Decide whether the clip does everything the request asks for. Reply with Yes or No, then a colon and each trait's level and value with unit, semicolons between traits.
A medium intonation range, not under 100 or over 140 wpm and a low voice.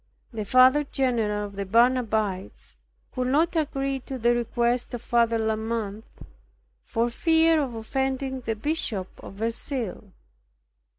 No: average, 3.3 semitones; slow, 135 wpm; high, 240 Hz